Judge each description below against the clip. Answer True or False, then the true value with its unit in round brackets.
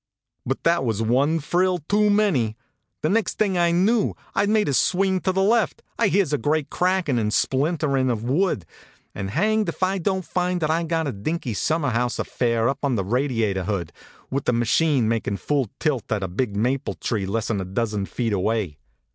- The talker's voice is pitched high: False (140 Hz)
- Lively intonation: True (8.1 semitones)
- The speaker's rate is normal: False (215 wpm)